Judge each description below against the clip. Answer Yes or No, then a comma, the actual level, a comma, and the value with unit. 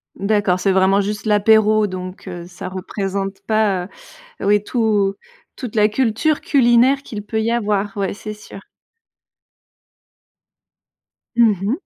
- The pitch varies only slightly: Yes, narrow, 2.1 semitones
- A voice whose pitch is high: Yes, high, 210 Hz